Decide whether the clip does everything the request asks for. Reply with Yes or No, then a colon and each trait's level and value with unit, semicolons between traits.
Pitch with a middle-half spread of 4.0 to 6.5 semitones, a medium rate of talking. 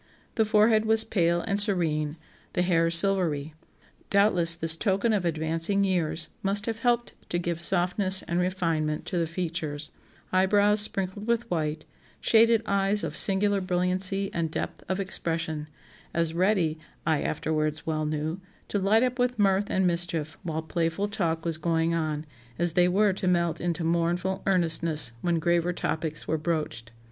No: average, 3.4 semitones; average, 155 wpm